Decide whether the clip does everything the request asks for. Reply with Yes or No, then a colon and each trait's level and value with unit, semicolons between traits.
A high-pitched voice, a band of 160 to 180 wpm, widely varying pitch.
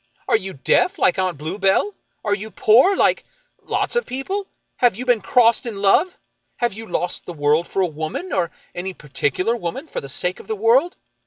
No: high, 205 Hz; average, 200 wpm; wide, 5.8 semitones